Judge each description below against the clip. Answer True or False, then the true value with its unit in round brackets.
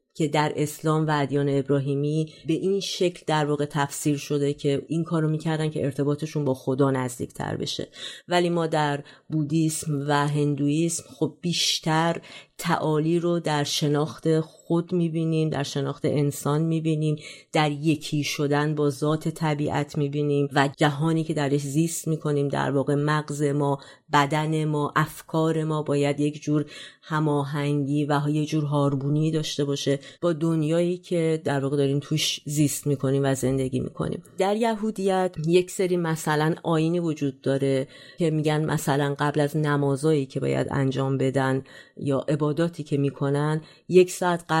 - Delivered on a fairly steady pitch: True (2.0 semitones)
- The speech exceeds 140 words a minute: True (150 wpm)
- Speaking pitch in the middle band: True (150 Hz)